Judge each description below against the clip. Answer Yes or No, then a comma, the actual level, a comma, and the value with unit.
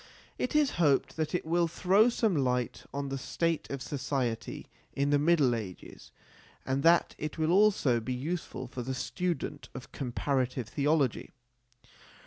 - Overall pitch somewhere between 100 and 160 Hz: Yes, medium, 140 Hz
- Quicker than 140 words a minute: Yes, average, 150 wpm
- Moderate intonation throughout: Yes, average, 4.7 semitones